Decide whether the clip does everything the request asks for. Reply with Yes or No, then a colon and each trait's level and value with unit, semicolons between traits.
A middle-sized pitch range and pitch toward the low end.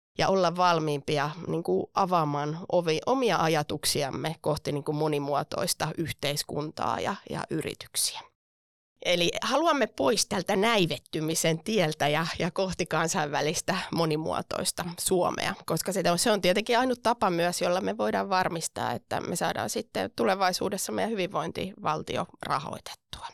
No: average, 3.4 semitones; medium, 170 Hz